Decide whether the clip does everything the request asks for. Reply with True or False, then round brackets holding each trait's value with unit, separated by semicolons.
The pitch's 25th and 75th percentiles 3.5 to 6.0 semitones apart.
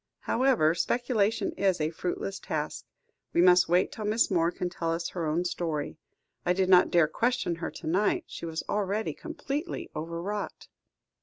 True (3.9 semitones)